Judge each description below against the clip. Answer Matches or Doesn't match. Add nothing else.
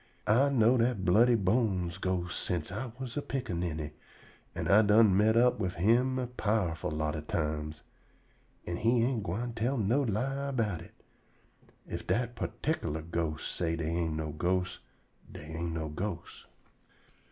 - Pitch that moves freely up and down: Matches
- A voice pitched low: Matches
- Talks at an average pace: Matches